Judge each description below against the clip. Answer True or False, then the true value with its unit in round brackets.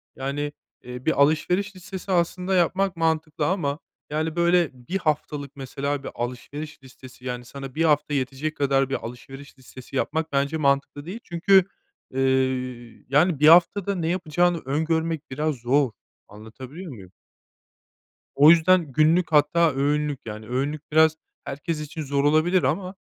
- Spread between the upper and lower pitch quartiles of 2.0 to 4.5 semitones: True (3.6 semitones)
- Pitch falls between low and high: True (150 Hz)